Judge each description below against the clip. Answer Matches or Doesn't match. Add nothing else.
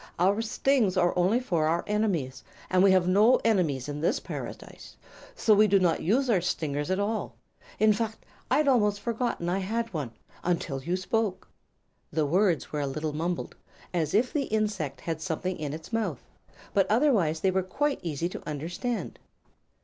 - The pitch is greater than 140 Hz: Matches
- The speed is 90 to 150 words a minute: Doesn't match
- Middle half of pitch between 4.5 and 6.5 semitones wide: Matches